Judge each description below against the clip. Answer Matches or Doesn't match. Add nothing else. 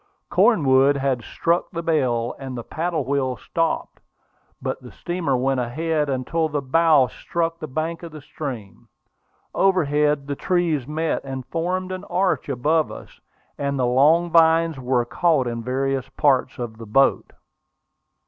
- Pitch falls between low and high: Matches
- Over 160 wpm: Doesn't match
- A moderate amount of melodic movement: Matches